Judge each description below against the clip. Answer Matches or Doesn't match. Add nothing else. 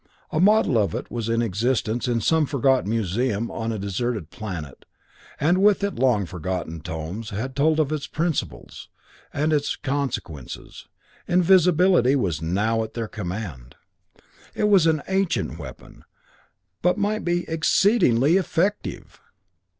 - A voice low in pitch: Matches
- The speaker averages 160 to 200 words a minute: Doesn't match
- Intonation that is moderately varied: Doesn't match